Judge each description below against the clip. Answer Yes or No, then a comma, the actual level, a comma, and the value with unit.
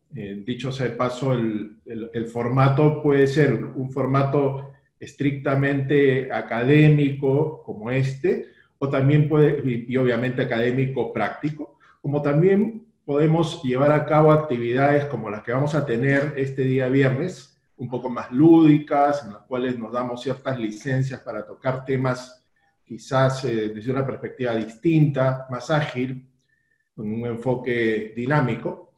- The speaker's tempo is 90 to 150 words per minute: Yes, average, 140 wpm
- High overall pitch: No, low, 135 Hz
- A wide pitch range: No, average, 2.7 semitones